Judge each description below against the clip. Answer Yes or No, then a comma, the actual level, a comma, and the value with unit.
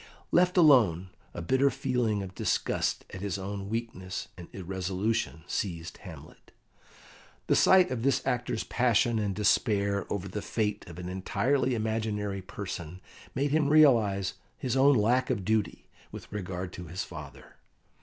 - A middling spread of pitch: Yes, average, 4.8 semitones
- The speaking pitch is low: Yes, low, 105 Hz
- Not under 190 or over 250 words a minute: No, average, 145 wpm